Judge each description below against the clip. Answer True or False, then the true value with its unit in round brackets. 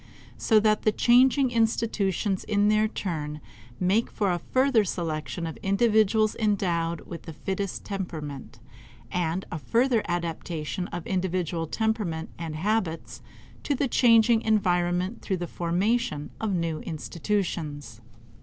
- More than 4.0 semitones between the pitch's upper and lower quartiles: True (4.6 semitones)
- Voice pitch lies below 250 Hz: True (190 Hz)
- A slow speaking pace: True (125 wpm)